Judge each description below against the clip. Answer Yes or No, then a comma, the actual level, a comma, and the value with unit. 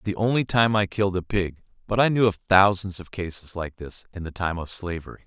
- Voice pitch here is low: Yes, very low, 95 Hz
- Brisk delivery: Yes, fast, 260 wpm